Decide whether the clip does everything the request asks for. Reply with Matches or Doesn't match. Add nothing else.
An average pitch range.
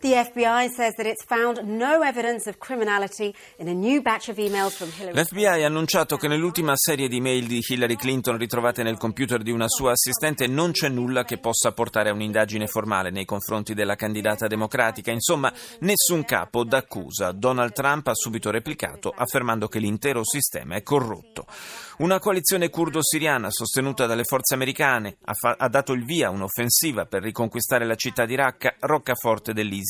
Doesn't match